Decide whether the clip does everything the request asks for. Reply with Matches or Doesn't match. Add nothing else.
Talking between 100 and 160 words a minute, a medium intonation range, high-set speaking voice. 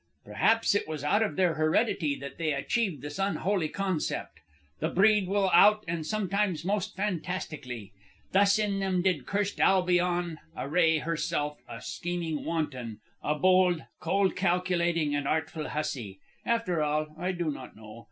Doesn't match